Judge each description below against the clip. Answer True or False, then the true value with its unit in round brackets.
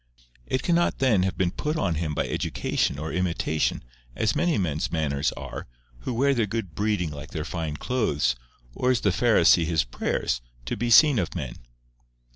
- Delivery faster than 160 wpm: True (180 wpm)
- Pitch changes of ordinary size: False (7.4 semitones)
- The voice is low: True (90 Hz)